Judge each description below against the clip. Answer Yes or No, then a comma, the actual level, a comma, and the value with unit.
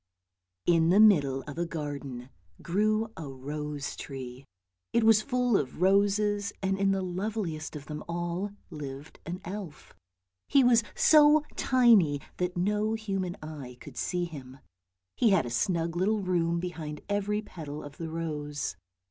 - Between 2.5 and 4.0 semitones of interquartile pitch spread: No, wide, 5.6 semitones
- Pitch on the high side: No, medium, 175 Hz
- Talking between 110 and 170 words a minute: Yes, average, 150 wpm